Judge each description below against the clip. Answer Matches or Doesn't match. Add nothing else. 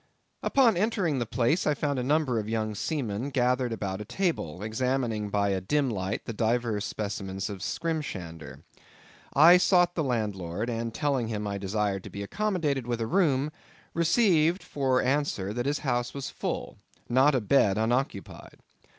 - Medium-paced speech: Matches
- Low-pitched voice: Matches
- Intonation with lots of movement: Matches